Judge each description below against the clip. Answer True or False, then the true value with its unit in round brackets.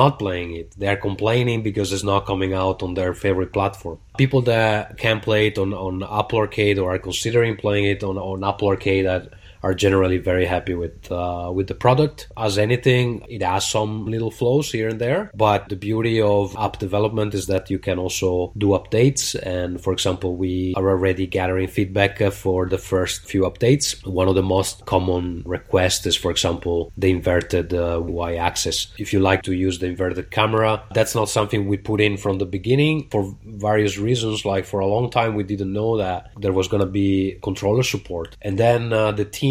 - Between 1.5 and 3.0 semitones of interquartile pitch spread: True (2.6 semitones)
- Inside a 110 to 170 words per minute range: False (200 wpm)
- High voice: False (100 Hz)